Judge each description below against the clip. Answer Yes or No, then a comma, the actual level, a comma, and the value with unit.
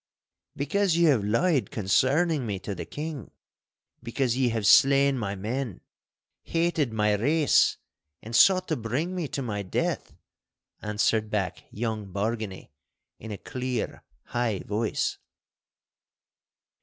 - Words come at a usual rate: No, slow, 125 wpm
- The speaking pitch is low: Yes, low, 115 Hz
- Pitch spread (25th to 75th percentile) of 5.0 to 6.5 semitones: Yes, average, 5.3 semitones